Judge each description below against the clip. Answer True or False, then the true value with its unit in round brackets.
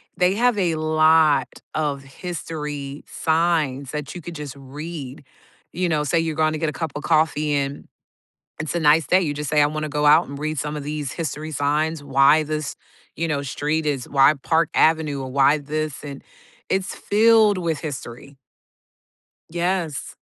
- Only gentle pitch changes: True (2.2 semitones)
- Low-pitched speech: False (155 Hz)